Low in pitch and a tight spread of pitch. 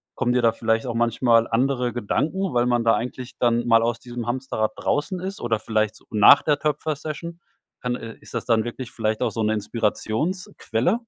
No: low, 120 Hz; average, 3.3 semitones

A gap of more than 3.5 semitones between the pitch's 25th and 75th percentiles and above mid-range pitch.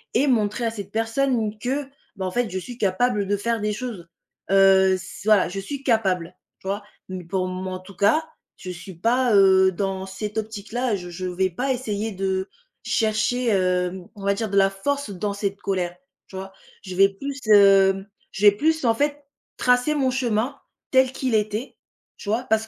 Yes: average, 4.1 semitones; high, 205 Hz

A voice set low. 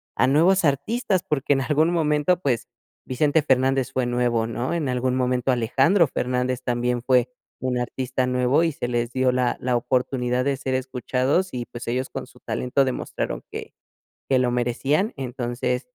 Yes: low, 130 Hz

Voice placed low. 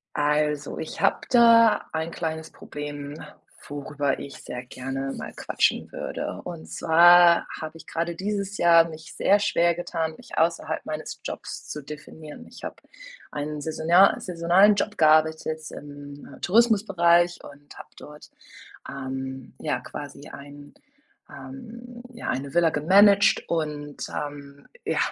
No: medium, 160 Hz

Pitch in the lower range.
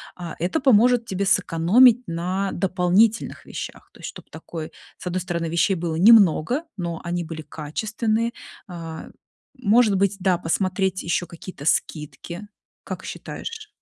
No: medium, 185 Hz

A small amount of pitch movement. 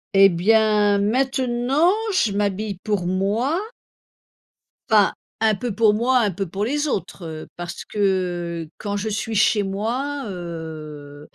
No: average, 3.9 semitones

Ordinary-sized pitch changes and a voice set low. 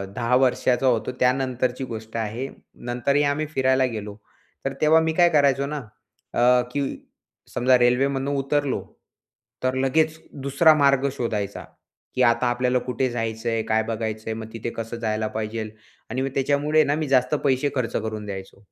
Yes: average, 3.4 semitones; low, 125 Hz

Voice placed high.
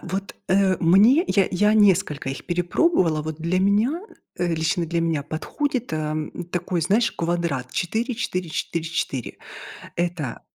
No: medium, 175 Hz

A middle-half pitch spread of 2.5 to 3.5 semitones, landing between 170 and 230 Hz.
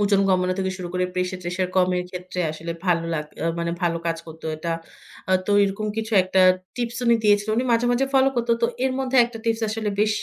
No: average, 4.1 semitones; high, 190 Hz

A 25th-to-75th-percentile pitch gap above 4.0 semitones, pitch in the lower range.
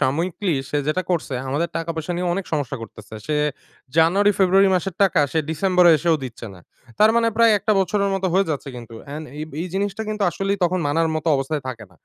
No: average, 4.5 semitones; medium, 170 Hz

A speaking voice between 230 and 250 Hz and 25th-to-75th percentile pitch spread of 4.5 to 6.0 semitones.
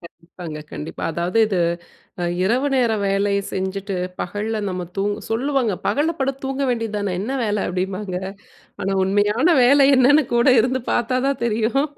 No: high, 215 Hz; average, 4.9 semitones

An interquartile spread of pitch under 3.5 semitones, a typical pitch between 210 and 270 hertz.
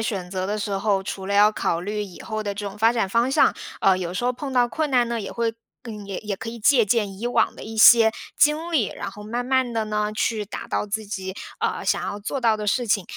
Yes: average, 2.8 semitones; high, 215 Hz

